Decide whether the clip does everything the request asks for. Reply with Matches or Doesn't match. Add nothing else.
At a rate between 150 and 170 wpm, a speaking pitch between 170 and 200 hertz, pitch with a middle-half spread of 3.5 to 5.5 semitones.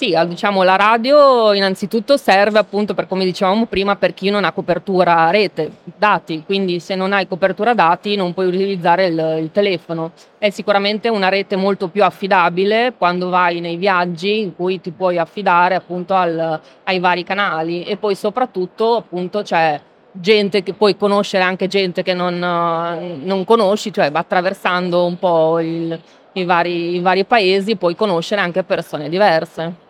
Doesn't match